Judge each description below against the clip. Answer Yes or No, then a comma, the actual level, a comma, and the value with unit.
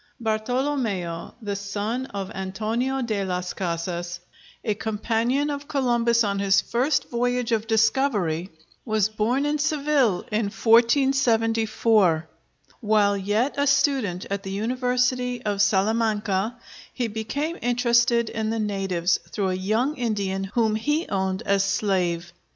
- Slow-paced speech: Yes, slow, 130 wpm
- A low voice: No, high, 220 Hz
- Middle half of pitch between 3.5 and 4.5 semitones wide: Yes, average, 3.9 semitones